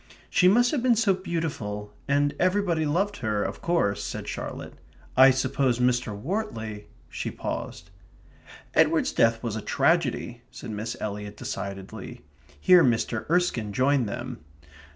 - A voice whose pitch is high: No, low, 130 Hz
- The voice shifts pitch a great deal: Yes, wide, 8.0 semitones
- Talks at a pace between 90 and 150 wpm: Yes, average, 140 wpm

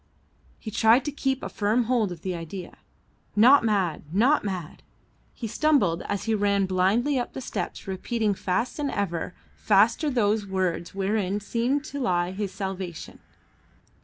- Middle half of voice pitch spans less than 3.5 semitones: No, average, 4.3 semitones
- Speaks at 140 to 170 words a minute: Yes, average, 155 wpm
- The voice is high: Yes, high, 205 Hz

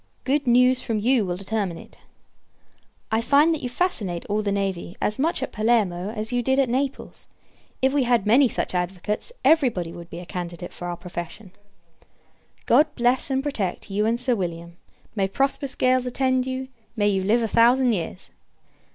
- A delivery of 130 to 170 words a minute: No, average, 185 wpm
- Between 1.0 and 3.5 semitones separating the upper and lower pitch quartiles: No, wide, 5.4 semitones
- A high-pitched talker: Yes, high, 225 Hz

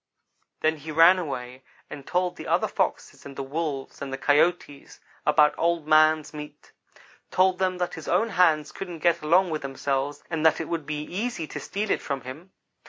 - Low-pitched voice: No, medium, 155 Hz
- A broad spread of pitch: No, average, 3.3 semitones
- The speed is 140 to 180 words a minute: No, average, 190 wpm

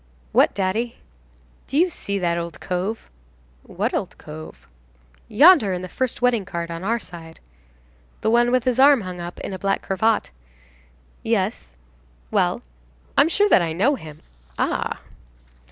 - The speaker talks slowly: No, average, 155 wpm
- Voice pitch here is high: Yes, high, 195 Hz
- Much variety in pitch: Yes, wide, 6.0 semitones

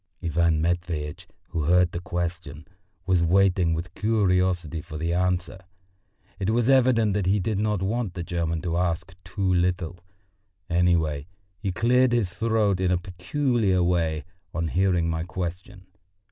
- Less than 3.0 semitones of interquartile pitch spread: Yes, narrow, 2.6 semitones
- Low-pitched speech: Yes, very low, 90 Hz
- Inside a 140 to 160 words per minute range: Yes, average, 145 wpm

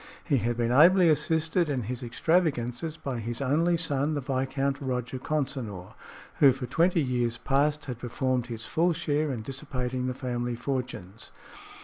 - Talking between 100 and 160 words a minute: Yes, average, 155 wpm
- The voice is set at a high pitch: No, low, 135 Hz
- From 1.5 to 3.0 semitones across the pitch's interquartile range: No, average, 3.7 semitones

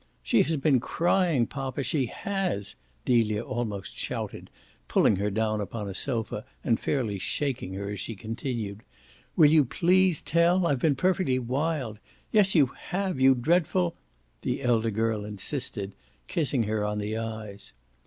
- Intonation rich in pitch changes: Yes, wide, 6.5 semitones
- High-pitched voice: No, low, 120 Hz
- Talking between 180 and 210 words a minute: No, average, 155 wpm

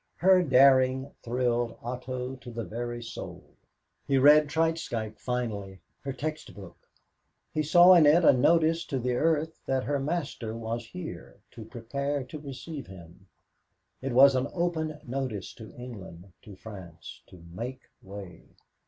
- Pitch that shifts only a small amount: No, average, 4.7 semitones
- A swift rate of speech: No, average, 145 wpm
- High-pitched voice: No, low, 130 Hz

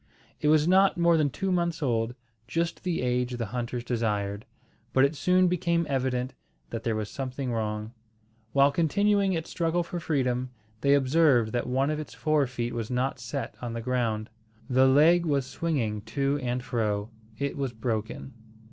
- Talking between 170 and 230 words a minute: Yes, average, 175 wpm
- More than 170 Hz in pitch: No, low, 130 Hz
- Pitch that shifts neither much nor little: Yes, average, 4.9 semitones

